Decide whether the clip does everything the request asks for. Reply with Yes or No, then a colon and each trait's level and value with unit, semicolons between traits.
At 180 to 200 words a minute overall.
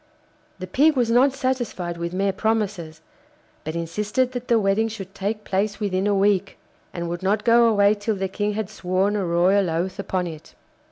Yes: average, 185 wpm